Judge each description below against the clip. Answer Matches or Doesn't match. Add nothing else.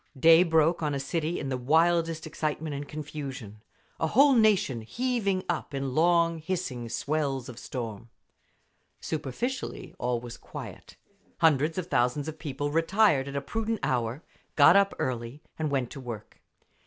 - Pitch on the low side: Doesn't match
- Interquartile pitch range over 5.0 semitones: Doesn't match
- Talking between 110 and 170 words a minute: Matches